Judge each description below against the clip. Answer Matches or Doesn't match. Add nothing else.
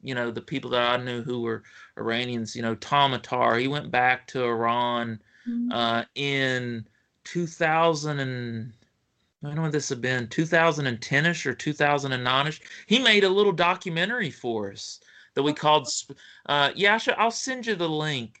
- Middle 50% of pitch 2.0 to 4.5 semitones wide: Doesn't match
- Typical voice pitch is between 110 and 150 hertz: Matches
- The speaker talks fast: Matches